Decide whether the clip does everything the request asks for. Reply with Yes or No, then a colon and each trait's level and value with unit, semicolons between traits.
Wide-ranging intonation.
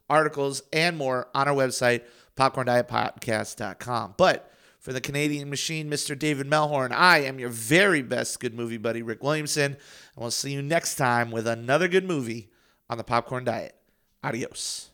No: average, 3.8 semitones